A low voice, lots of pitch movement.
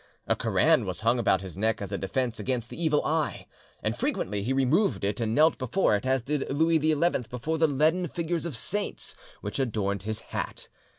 Yes: low, 130 Hz; wide, 6.4 semitones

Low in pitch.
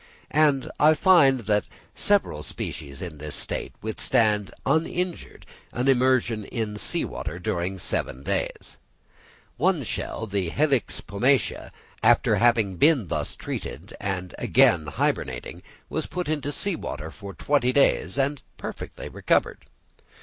Yes: low, 115 Hz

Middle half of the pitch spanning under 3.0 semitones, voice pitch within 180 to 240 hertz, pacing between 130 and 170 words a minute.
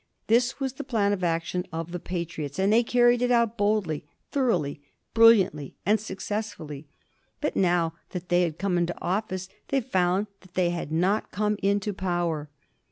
No: average, 4.0 semitones; high, 190 Hz; average, 165 wpm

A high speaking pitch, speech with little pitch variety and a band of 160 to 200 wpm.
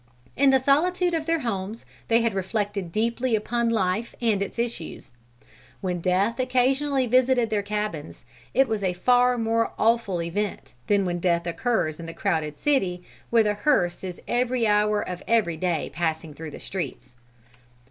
No: high, 210 Hz; average, 5.3 semitones; average, 165 wpm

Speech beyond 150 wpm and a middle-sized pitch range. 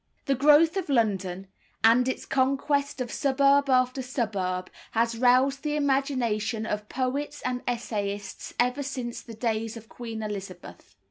No: average, 140 wpm; average, 4.0 semitones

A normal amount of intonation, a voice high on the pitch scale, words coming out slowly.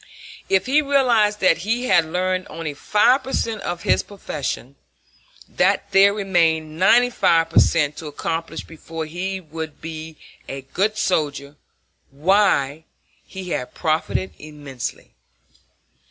No: average, 4.4 semitones; medium, 165 Hz; slow, 130 wpm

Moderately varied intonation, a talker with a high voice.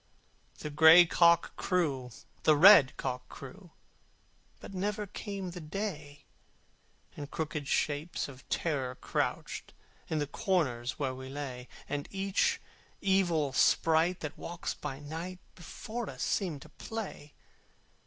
No: average, 4.4 semitones; medium, 160 Hz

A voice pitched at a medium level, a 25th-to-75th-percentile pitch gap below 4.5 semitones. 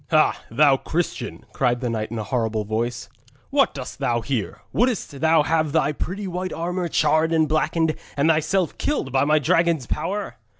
No: medium, 155 Hz; average, 5.2 semitones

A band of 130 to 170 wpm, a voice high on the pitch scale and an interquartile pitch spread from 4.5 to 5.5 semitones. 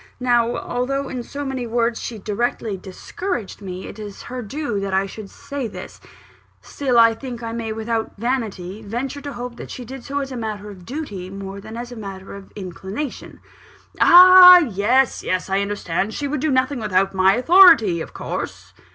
No: average, 185 wpm; high, 230 Hz; average, 5.0 semitones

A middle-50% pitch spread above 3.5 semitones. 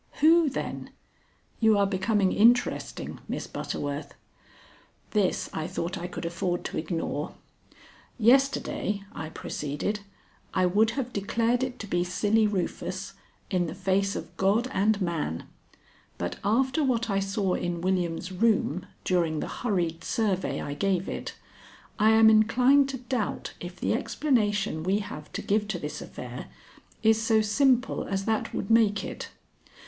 Yes: average, 4.0 semitones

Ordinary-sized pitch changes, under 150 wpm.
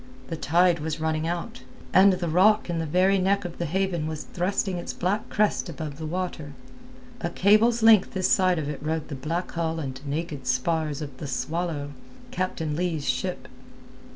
No: average, 3.4 semitones; average, 180 wpm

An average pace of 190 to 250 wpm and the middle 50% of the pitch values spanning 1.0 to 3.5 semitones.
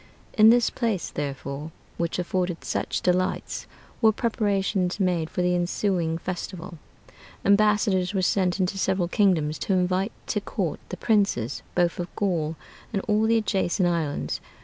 No: average, 145 wpm; average, 2.9 semitones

